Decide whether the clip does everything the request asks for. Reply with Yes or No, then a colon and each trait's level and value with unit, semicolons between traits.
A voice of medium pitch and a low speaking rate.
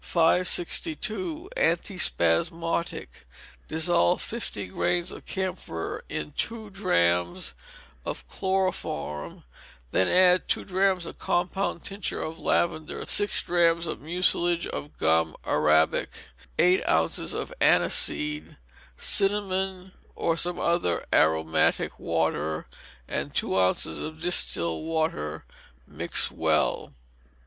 Yes: medium, 170 Hz; slow, 105 wpm